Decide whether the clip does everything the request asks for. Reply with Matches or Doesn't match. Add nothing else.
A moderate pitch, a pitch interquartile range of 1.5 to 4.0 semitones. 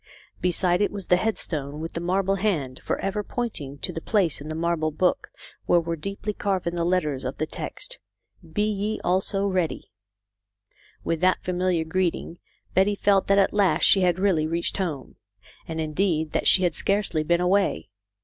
Matches